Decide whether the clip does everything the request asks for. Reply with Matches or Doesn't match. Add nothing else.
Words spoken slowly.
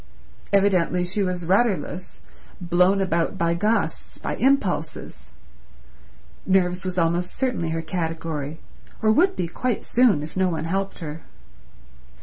Matches